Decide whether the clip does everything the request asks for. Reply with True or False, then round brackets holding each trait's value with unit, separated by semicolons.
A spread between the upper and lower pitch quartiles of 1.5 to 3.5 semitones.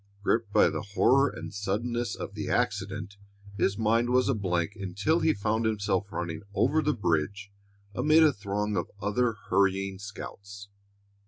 True (3.0 semitones)